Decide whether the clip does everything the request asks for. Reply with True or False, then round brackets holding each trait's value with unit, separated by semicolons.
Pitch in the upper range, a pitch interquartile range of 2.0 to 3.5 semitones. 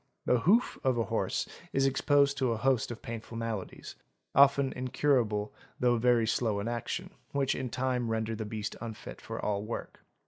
False (120 Hz; 3.2 semitones)